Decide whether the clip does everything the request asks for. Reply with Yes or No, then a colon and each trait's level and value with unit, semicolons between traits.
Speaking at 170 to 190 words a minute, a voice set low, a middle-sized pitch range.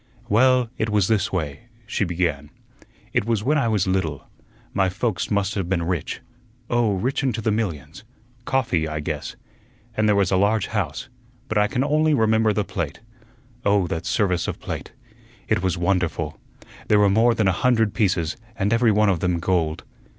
Yes: average, 180 wpm; low, 100 Hz; average, 4.1 semitones